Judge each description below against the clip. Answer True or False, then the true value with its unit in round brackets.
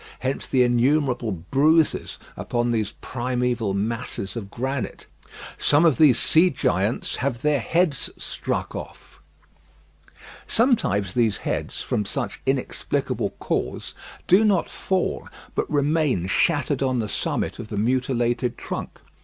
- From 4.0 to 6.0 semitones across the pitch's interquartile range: True (4.3 semitones)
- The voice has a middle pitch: False (125 Hz)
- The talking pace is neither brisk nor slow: False (125 wpm)